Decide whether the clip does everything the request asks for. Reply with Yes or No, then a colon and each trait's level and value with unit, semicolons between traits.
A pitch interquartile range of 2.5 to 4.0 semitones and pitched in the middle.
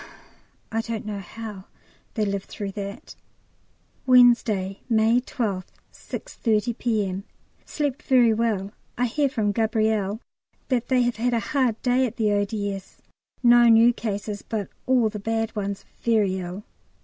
No: average, 2.8 semitones; high, 220 Hz